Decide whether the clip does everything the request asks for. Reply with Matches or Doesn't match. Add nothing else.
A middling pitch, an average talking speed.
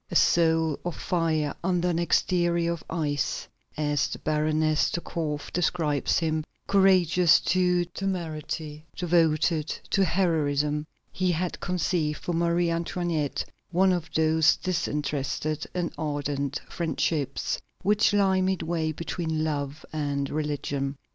Doesn't match